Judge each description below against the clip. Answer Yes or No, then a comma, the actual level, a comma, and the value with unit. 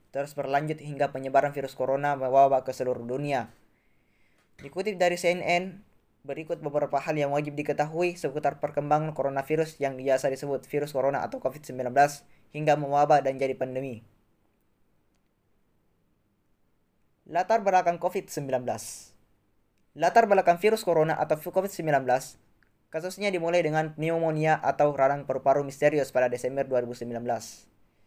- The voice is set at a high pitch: No, medium, 140 Hz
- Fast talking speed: No, average, 115 wpm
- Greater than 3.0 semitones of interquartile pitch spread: Yes, average, 3.4 semitones